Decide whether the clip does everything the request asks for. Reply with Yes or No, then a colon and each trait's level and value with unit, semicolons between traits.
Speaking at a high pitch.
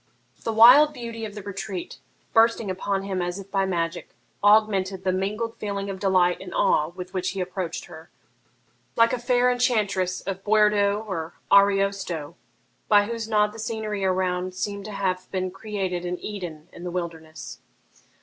Yes: high, 195 Hz